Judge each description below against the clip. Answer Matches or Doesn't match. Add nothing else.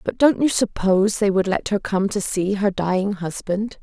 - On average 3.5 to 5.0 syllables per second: Matches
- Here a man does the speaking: Doesn't match